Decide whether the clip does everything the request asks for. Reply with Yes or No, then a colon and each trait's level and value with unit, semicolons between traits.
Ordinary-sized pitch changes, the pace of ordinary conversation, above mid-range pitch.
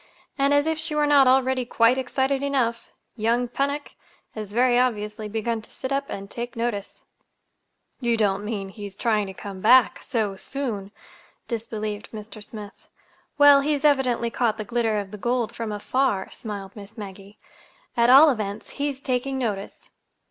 Yes: average, 4.0 semitones; average, 165 wpm; high, 235 Hz